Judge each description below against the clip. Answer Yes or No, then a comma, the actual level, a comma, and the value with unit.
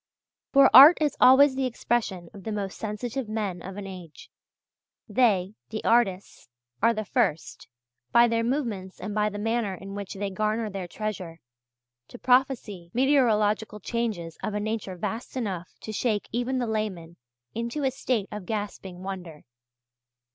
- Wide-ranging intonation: No, average, 3.7 semitones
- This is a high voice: Yes, high, 215 Hz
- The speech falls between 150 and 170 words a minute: Yes, average, 155 wpm